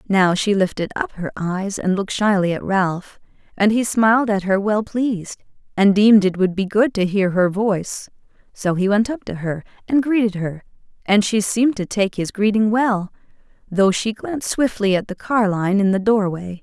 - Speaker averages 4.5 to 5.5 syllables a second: Yes, 5.0 syllables/s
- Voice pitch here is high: Yes, high, 205 Hz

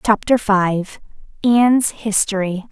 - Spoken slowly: Yes, slow, 90 wpm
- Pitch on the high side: Yes, high, 205 Hz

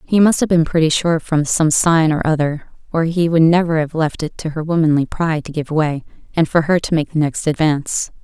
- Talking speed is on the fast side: Yes, fast, 240 wpm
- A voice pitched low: No, medium, 160 Hz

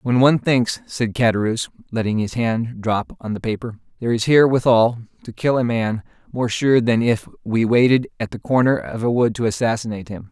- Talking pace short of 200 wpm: No, fast, 205 wpm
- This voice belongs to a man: Yes, male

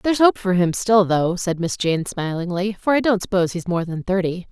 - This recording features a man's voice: No, female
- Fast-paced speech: Yes, fast, 240 wpm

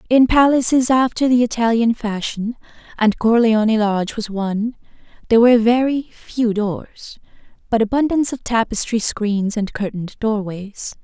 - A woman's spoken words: Yes, female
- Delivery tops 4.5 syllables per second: Yes, 4.9 syllables/s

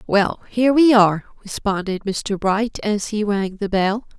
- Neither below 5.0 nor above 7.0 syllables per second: No, 4.3 syllables/s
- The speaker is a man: No, female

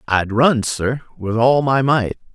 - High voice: No, low, 120 Hz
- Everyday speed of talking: Yes, average, 180 wpm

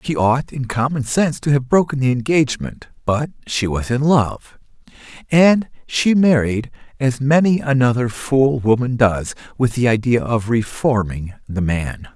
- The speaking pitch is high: No, low, 125 Hz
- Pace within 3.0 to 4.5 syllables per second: Yes, 4.4 syllables/s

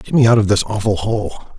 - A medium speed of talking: No, fast, 265 wpm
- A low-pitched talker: Yes, low, 110 Hz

